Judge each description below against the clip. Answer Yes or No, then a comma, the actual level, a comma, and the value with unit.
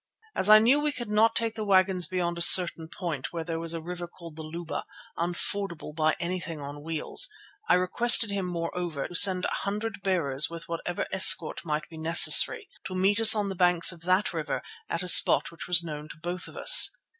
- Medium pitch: Yes, medium, 175 Hz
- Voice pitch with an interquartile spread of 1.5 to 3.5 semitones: Yes, average, 2.8 semitones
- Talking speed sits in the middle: No, fast, 210 wpm